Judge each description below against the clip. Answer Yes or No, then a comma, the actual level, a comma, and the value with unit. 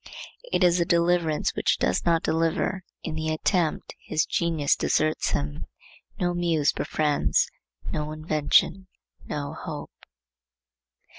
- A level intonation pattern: Yes, narrow, 2.0 semitones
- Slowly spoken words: Yes, slow, 120 wpm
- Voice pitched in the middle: Yes, medium, 160 Hz